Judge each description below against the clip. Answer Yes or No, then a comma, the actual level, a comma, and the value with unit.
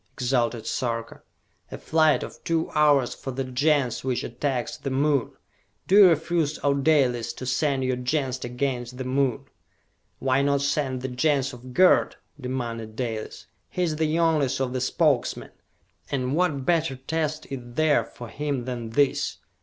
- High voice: No, low, 135 Hz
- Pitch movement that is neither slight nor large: Yes, average, 3.3 semitones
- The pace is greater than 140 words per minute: Yes, average, 160 wpm